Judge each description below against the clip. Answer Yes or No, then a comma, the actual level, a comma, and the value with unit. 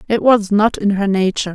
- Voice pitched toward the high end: Yes, high, 205 Hz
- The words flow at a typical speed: No, fast, 235 wpm